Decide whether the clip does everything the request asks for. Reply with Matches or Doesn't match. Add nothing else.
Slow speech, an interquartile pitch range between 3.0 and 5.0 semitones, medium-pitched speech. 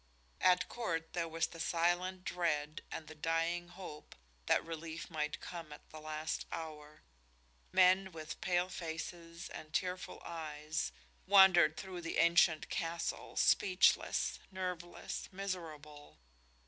Doesn't match